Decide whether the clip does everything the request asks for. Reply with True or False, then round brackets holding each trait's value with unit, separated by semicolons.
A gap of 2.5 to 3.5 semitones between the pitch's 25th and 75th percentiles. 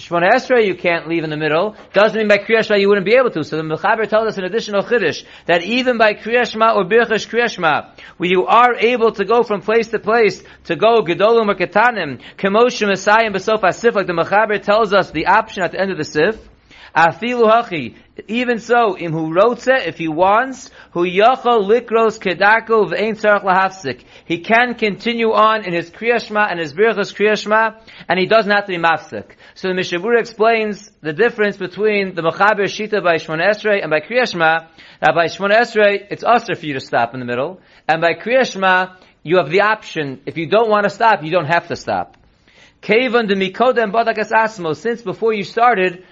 False (4.4 semitones)